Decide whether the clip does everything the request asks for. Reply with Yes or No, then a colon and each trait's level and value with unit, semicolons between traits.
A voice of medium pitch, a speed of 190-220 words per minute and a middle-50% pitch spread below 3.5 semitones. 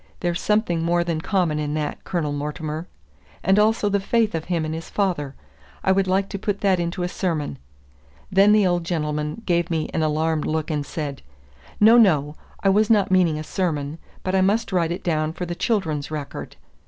No: medium, 170 Hz; average, 200 wpm; average, 3.8 semitones